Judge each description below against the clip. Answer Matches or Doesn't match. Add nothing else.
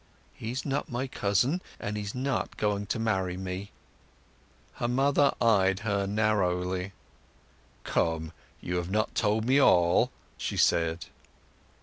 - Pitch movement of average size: Matches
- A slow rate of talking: Matches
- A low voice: Matches